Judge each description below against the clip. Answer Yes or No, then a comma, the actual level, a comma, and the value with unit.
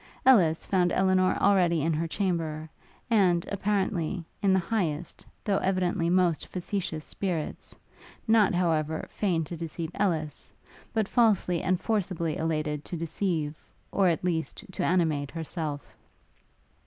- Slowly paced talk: Yes, slow, 130 wpm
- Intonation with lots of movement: No, average, 3.1 semitones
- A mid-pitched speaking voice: Yes, medium, 175 Hz